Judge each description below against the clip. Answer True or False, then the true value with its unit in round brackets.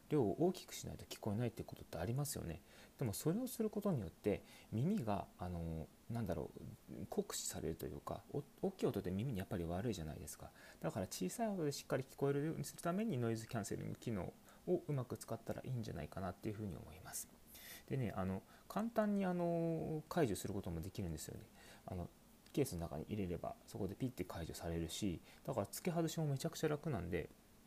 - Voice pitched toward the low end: True (115 Hz)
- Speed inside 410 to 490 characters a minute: True (435 characters per minute)